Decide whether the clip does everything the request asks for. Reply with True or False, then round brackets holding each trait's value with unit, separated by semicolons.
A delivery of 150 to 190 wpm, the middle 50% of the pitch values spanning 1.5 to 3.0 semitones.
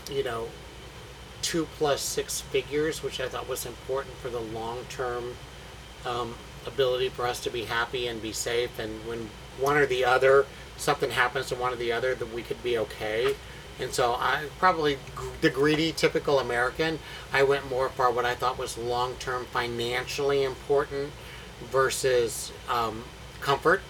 True (160 wpm; 2.6 semitones)